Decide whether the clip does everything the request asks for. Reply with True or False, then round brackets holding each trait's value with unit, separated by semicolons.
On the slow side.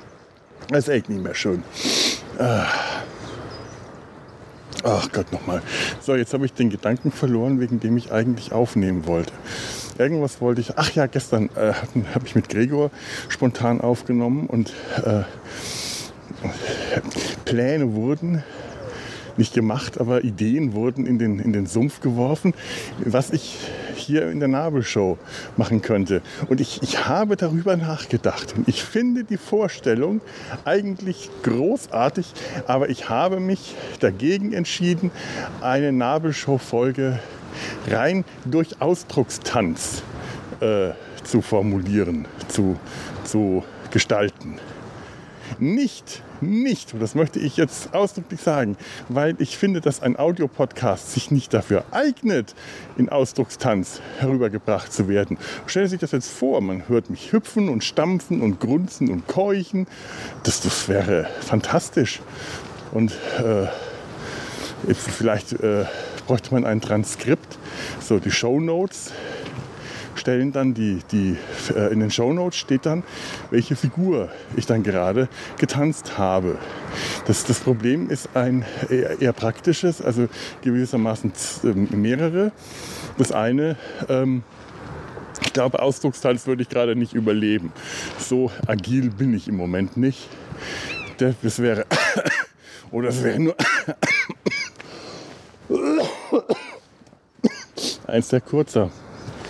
True (120 wpm)